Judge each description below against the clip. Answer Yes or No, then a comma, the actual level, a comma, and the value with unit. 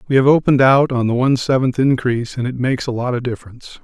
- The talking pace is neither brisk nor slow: No, fast, 250 wpm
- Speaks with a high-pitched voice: No, low, 125 Hz